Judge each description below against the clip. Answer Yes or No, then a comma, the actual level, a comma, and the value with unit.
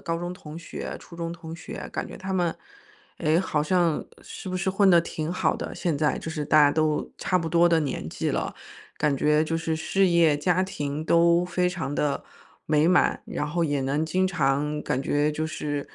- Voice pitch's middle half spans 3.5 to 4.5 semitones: No, average, 2.7 semitones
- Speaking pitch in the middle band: Yes, medium, 160 Hz